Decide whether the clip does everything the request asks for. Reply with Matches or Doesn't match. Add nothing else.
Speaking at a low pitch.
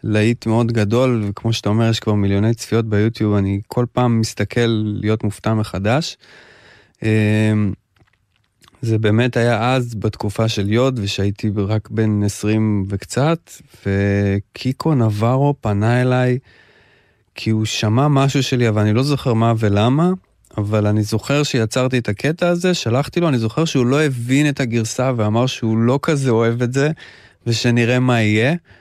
Matches